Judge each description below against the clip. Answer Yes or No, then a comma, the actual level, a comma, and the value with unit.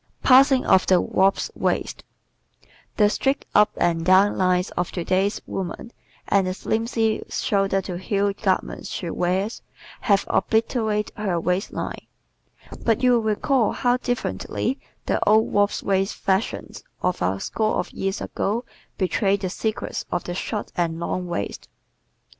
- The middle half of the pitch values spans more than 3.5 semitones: No, average, 3.2 semitones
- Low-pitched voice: No, high, 195 Hz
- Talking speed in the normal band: Yes, average, 145 wpm